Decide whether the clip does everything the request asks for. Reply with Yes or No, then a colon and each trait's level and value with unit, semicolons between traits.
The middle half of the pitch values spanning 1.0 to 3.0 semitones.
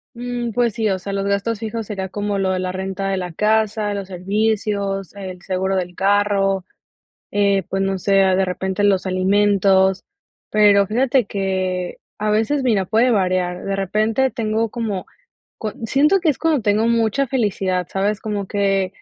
Yes: narrow, 2.4 semitones